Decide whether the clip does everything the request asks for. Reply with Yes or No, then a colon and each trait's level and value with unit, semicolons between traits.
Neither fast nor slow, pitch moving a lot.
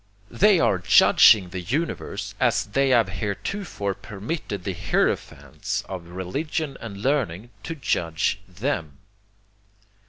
No: slow, 115 wpm; wide, 7.3 semitones